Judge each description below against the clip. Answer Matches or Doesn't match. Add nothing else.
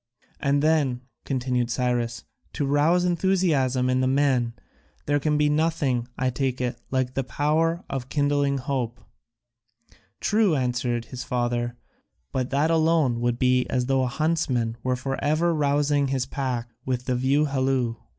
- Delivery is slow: Doesn't match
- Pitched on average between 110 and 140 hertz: Matches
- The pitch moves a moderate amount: Matches